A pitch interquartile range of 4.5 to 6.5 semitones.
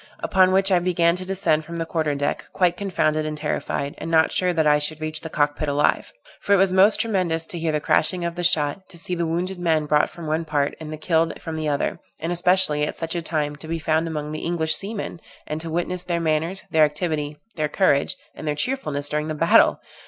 No: narrow, 2.6 semitones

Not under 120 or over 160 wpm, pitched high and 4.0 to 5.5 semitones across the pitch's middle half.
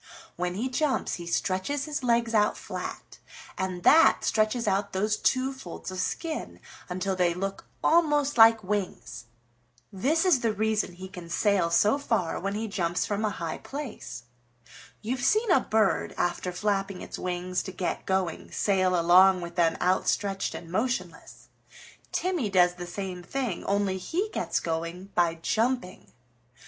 Yes: average, 155 wpm; high, 195 Hz; average, 4.7 semitones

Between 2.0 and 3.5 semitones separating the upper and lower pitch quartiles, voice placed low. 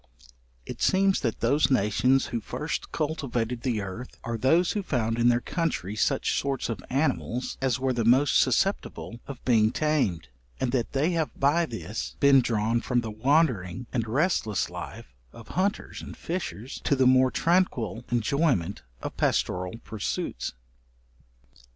No: average, 4.5 semitones; low, 125 Hz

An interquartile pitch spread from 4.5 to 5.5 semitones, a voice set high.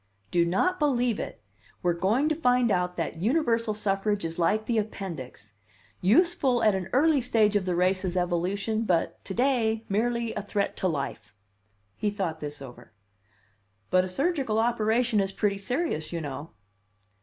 Yes: average, 5.1 semitones; high, 205 Hz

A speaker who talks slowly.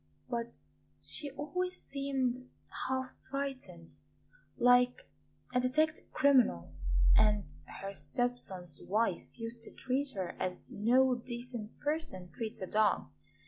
Yes: slow, 115 wpm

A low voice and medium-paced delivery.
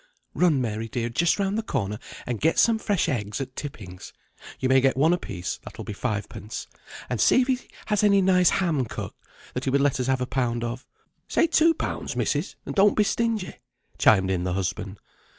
No: low, 130 Hz; fast, 215 wpm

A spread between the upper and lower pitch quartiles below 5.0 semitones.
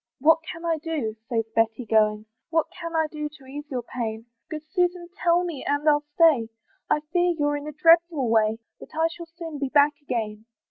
No: wide, 5.4 semitones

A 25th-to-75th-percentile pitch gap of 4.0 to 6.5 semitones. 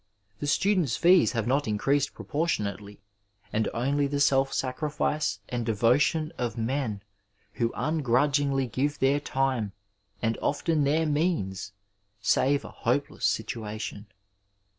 Yes: average, 4.3 semitones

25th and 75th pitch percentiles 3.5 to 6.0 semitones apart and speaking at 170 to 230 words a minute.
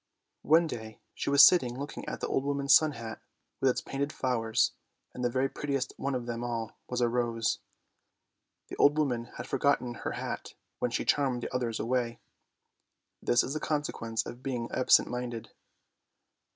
No: average, 2.9 semitones; average, 175 wpm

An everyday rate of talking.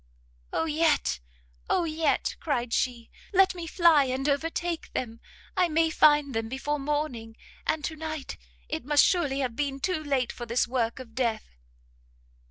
Yes: average, 160 wpm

